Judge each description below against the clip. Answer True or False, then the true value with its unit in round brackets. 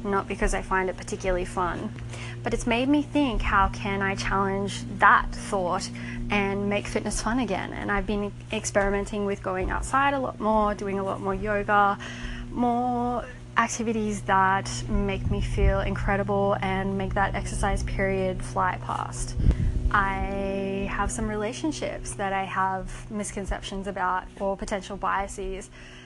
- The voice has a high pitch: True (195 Hz)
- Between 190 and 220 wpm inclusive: False (145 wpm)